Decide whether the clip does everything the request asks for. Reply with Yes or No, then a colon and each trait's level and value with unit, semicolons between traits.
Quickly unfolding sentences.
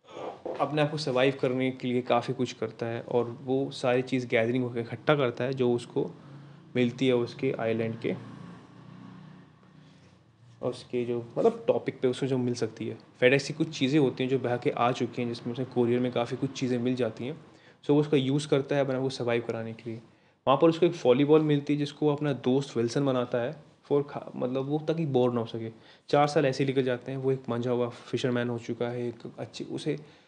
Yes: fast, 220 wpm